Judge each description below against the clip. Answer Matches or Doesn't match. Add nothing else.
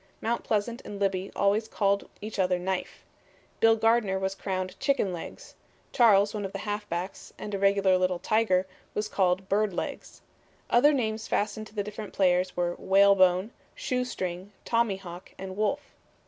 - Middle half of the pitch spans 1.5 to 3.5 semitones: Matches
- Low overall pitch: Doesn't match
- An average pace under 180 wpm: Matches